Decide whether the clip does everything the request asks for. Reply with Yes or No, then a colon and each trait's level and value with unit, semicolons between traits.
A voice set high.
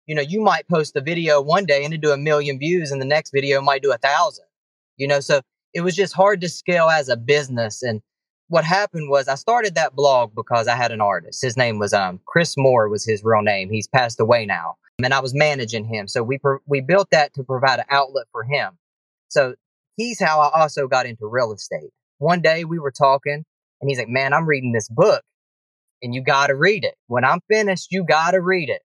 No: medium, 140 Hz